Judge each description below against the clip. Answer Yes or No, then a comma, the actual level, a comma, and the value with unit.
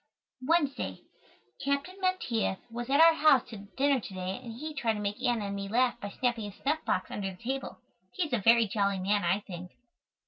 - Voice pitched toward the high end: Yes, high, 235 Hz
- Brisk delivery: Yes, fast, 210 wpm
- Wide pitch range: Yes, wide, 5.7 semitones